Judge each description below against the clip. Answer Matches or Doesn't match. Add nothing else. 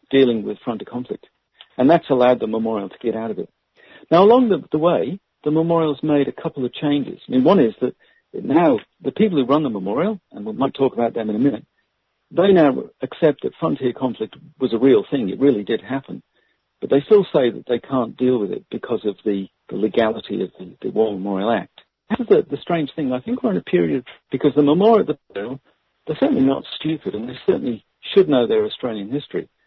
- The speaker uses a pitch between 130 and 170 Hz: Matches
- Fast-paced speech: Matches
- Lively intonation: Matches